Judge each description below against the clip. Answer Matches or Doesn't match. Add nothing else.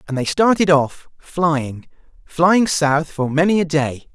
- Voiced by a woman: Doesn't match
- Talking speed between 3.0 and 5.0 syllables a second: Matches